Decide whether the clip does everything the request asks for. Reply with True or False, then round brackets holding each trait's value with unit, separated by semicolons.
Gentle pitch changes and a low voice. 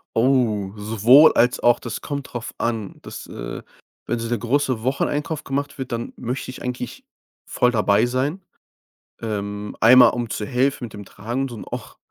False (3.2 semitones; 120 Hz)